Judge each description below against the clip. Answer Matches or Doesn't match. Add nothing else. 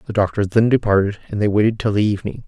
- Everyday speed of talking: Doesn't match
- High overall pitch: Doesn't match